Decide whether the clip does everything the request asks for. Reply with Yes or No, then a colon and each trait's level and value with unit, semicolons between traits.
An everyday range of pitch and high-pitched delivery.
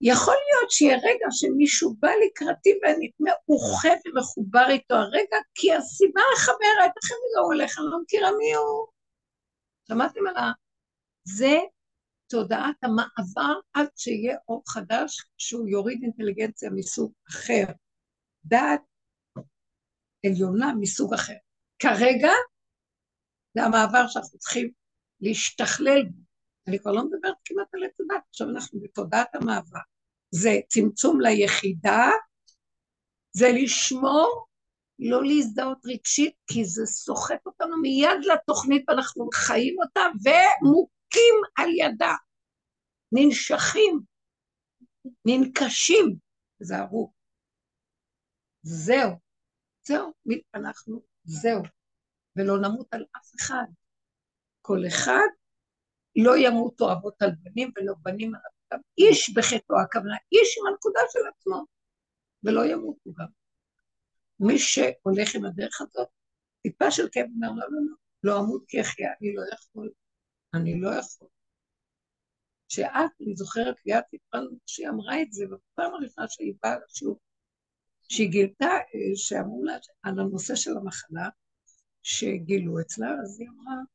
No: wide, 7.2 semitones; very high, 250 Hz